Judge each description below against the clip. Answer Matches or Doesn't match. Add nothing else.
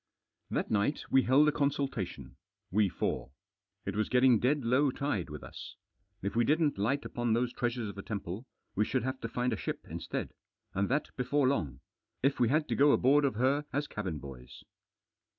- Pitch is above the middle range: Doesn't match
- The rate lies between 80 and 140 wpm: Doesn't match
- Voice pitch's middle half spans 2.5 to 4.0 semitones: Doesn't match